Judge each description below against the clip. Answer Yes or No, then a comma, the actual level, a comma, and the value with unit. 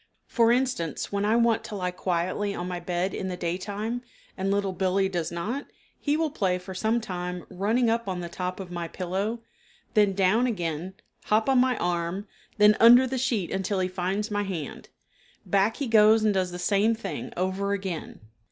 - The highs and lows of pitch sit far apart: No, average, 3.5 semitones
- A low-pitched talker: No, high, 195 Hz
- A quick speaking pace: No, average, 195 wpm